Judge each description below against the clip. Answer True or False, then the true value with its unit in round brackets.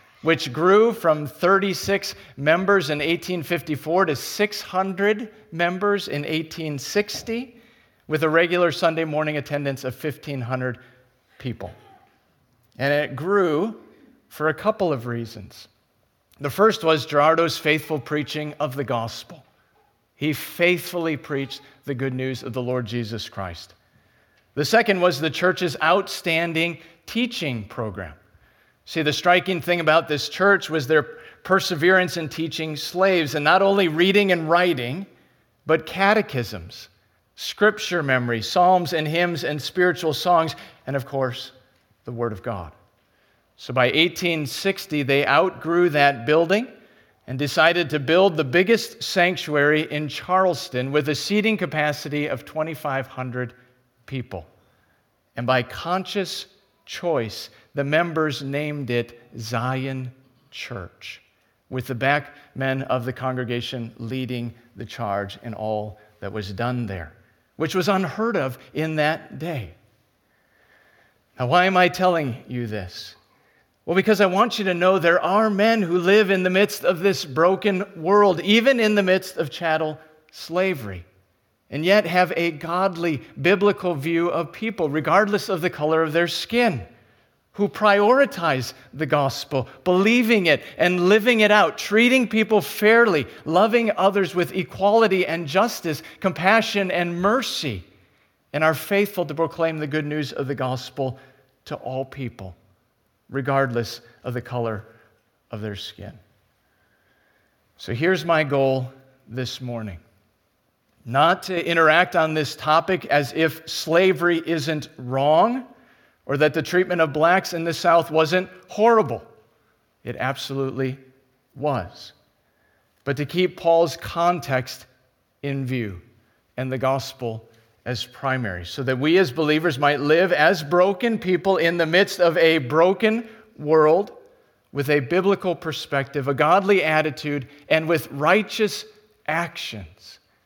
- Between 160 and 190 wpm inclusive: False (135 wpm)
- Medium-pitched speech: True (155 Hz)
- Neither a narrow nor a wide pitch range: False (5.9 semitones)